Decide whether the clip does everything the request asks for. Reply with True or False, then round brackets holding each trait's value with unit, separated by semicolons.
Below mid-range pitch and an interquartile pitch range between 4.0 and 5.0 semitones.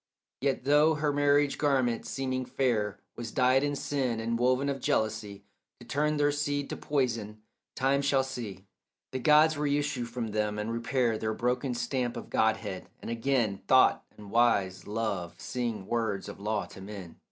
True (125 Hz; 4.3 semitones)